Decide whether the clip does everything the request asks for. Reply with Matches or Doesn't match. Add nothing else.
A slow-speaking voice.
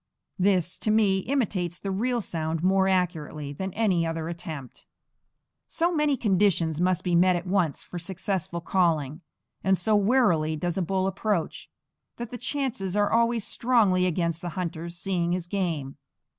Doesn't match